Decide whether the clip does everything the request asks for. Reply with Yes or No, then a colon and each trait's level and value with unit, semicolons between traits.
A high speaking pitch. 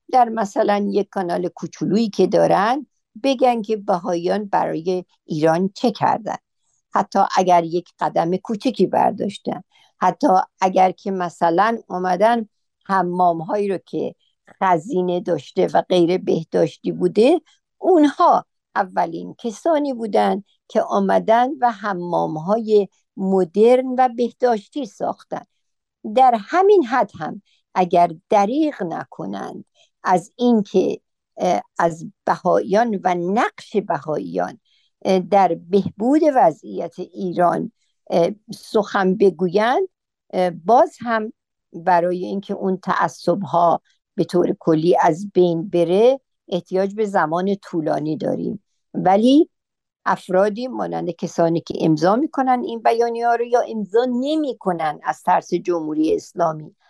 Yes: high, 195 Hz